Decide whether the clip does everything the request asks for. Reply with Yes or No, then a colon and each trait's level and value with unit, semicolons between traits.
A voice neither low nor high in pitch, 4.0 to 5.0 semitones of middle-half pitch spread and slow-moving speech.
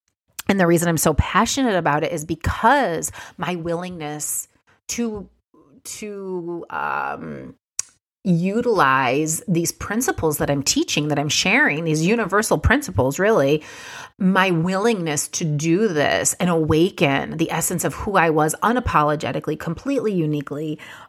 Yes: medium, 170 Hz; average, 4.7 semitones; slow, 125 wpm